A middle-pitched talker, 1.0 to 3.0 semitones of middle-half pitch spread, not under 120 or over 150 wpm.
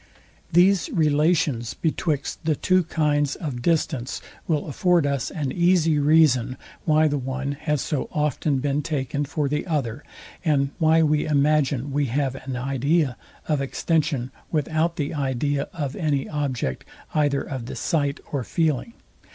Yes: medium, 145 Hz; narrow, 2.5 semitones; average, 145 wpm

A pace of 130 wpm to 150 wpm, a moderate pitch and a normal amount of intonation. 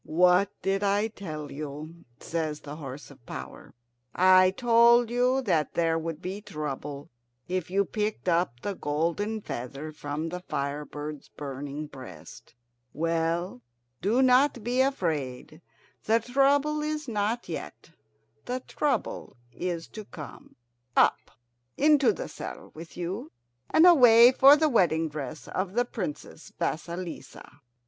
No: slow, 135 wpm; medium, 180 Hz; wide, 7.0 semitones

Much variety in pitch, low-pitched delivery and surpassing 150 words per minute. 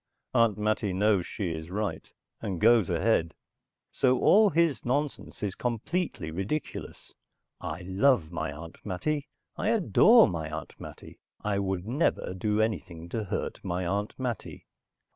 No: wide, 5.9 semitones; low, 105 Hz; average, 145 wpm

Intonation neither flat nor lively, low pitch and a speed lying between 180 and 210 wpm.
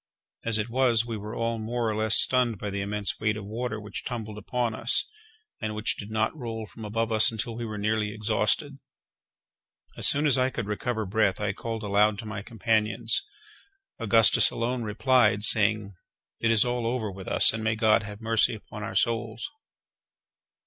No: narrow, 1.7 semitones; low, 110 Hz; average, 185 wpm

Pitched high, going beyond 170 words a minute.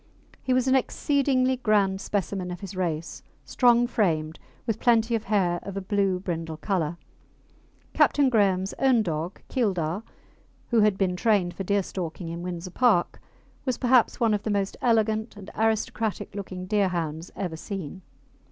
No: high, 200 Hz; average, 150 wpm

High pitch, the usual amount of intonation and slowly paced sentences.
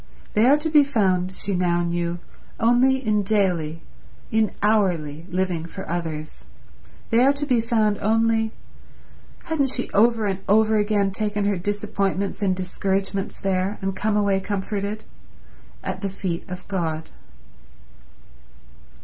Yes: high, 200 Hz; average, 3.0 semitones; slow, 130 wpm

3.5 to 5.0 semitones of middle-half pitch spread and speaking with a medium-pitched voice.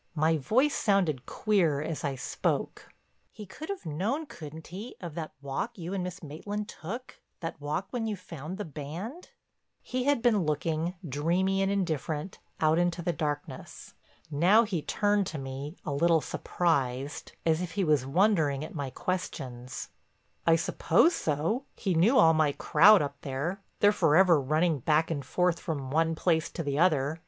Yes: average, 4.7 semitones; medium, 165 Hz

